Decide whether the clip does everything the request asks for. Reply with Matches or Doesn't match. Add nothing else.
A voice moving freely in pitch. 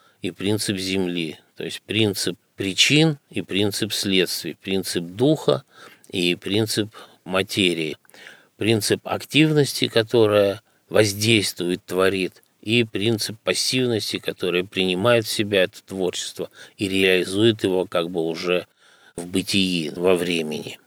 Doesn't match